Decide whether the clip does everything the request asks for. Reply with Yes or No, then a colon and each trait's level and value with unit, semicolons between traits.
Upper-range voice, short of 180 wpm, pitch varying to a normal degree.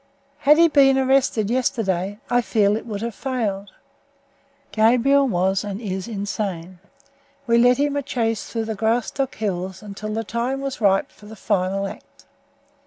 Yes: high, 220 Hz; average, 165 wpm; average, 4.1 semitones